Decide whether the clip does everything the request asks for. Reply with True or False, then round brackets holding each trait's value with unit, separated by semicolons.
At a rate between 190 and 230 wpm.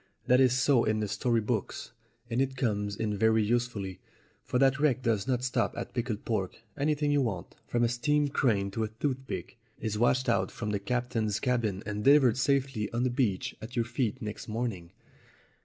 True (195 wpm)